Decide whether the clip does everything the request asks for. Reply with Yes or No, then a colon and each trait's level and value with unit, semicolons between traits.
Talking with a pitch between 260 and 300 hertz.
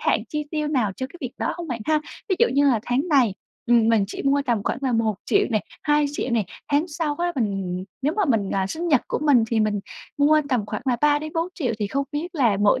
Yes: very high, 265 Hz